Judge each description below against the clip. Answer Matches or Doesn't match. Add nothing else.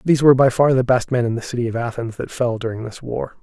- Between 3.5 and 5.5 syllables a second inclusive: Doesn't match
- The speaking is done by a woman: Doesn't match